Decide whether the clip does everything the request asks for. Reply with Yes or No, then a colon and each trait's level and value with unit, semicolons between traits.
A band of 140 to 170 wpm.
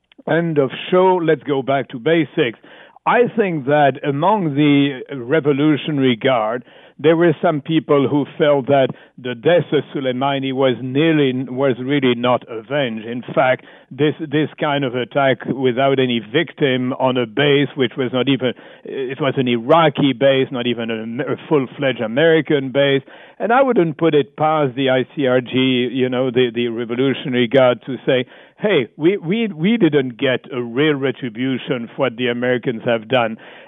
Yes: average, 160 wpm